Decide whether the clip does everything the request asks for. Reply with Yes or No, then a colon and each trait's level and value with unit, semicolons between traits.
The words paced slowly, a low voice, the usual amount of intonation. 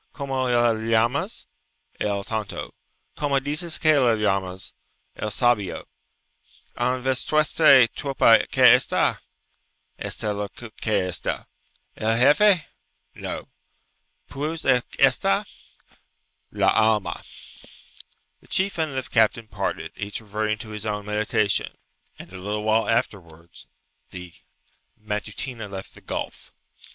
Yes: slow, 115 wpm; low, 110 Hz; average, 4.3 semitones